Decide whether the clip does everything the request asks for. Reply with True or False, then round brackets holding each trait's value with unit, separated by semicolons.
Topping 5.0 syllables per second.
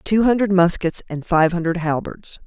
False (4.9 syllables/s)